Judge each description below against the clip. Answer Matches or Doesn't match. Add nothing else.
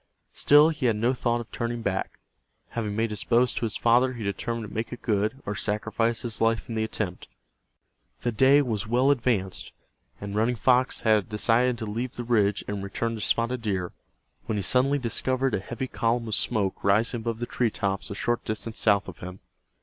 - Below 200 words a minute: Doesn't match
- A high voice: Doesn't match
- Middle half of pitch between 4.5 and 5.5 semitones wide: Doesn't match